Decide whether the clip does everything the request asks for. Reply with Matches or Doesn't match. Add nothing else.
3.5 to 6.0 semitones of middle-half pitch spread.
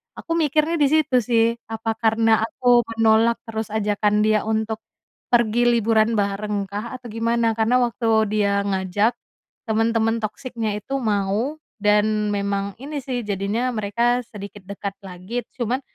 Doesn't match